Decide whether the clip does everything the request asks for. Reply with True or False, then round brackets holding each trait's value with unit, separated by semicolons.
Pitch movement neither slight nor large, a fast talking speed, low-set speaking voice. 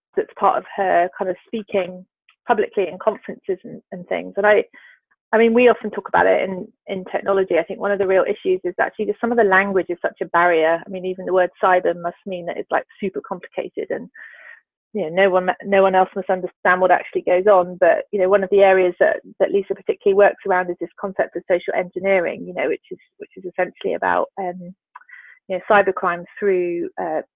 False (4.0 semitones; 225 wpm; 195 Hz)